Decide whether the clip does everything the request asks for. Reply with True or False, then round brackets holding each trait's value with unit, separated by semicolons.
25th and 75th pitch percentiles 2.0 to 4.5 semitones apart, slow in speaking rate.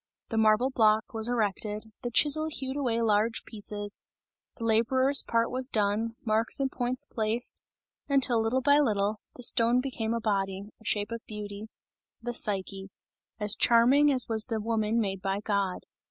False (2.8 semitones; 165 wpm)